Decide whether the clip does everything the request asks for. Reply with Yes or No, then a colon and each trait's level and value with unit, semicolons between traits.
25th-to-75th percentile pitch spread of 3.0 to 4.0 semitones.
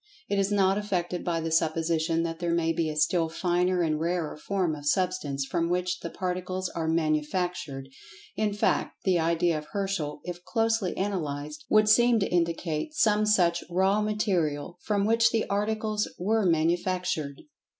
Yes: average, 3.5 semitones